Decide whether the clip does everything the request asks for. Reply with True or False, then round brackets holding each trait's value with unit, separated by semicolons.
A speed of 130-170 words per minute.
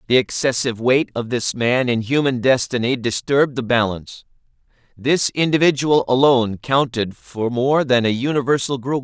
True (145 wpm)